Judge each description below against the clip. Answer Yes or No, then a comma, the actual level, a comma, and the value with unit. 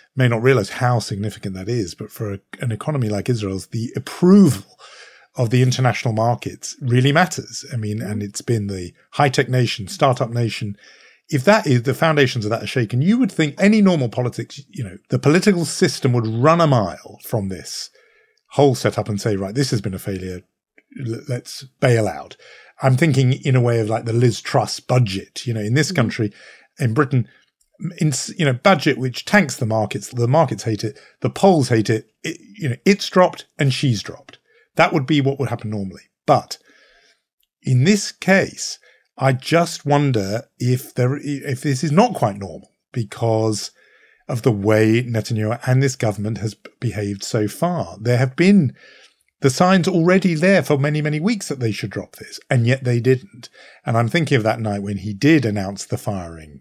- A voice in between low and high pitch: No, low, 125 Hz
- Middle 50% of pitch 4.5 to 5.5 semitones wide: Yes, average, 5.1 semitones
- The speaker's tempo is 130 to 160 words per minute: No, average, 190 wpm